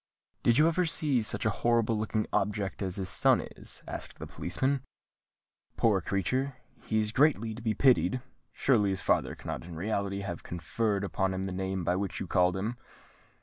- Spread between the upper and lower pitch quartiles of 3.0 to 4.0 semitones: Yes, average, 3.7 semitones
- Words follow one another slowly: No, average, 180 wpm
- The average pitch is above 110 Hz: No, low, 105 Hz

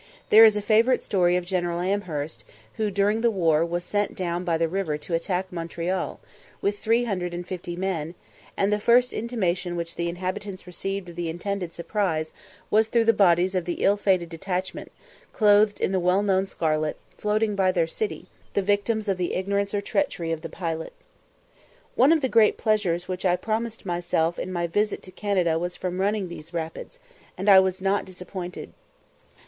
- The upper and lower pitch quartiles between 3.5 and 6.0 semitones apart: No, average, 3.0 semitones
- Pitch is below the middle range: No, medium, 185 Hz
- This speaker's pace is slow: No, average, 185 wpm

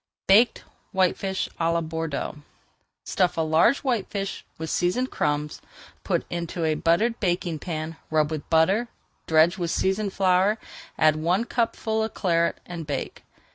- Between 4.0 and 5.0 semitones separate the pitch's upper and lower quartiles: No, average, 3.5 semitones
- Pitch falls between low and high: Yes, medium, 175 Hz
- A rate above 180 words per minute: No, average, 140 wpm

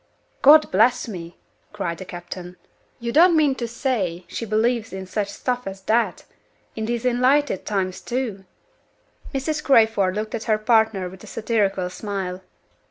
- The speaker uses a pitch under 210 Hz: No, high, 220 Hz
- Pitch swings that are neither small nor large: Yes, average, 4.4 semitones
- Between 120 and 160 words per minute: Yes, average, 155 wpm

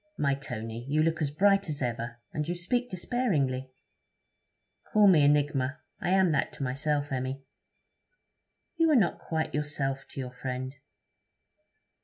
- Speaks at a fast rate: No, average, 145 wpm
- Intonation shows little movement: No, average, 4.8 semitones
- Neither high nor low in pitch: Yes, medium, 145 Hz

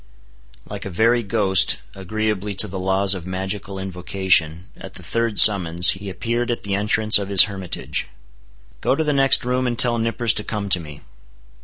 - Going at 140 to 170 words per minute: No, average, 180 wpm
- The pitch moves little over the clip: No, average, 3.3 semitones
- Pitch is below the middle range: Yes, low, 100 Hz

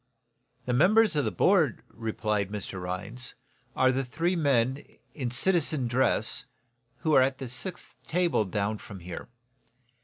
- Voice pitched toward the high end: No, low, 125 Hz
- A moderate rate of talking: Yes, average, 145 wpm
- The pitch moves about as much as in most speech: No, wide, 6.2 semitones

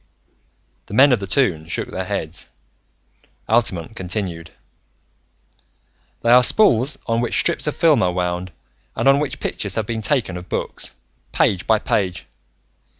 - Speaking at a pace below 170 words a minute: Yes, average, 150 wpm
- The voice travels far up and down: Yes, wide, 5.8 semitones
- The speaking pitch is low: Yes, low, 110 Hz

